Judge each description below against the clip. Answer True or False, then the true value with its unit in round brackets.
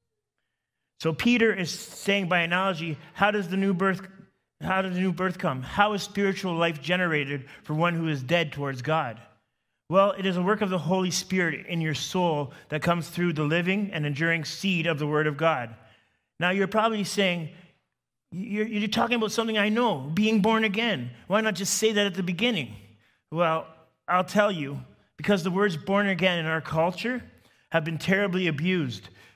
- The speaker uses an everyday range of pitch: True (4.0 semitones)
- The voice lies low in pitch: False (180 Hz)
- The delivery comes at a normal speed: True (190 wpm)